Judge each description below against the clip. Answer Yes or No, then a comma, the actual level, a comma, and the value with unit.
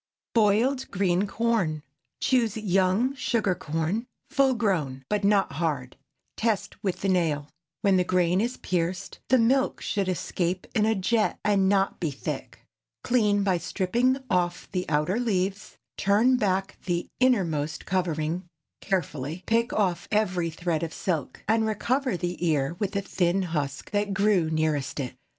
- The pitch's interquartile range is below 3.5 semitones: No, average, 4.2 semitones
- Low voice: No, high, 190 Hz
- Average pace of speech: Yes, average, 150 wpm